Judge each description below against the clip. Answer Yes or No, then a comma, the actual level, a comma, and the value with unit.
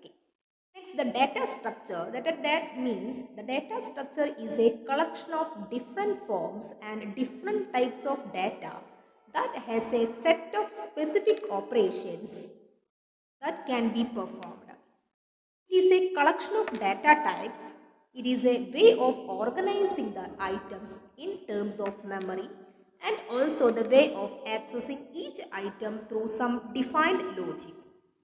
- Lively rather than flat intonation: Yes, wide, 6.9 semitones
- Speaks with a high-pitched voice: Yes, very high, 255 Hz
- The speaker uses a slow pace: Yes, slow, 130 wpm